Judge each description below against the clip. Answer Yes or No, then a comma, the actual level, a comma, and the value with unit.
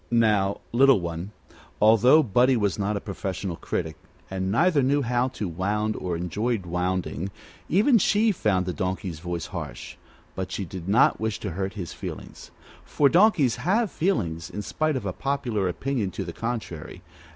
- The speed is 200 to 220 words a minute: No, average, 165 wpm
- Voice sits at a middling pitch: No, low, 105 Hz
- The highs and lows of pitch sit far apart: Yes, wide, 6.0 semitones